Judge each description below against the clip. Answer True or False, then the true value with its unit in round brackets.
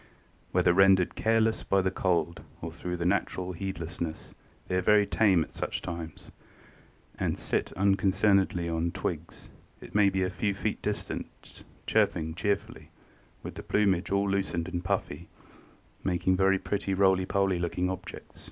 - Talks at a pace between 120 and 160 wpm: True (155 wpm)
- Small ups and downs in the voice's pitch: True (2.1 semitones)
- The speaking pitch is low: True (95 Hz)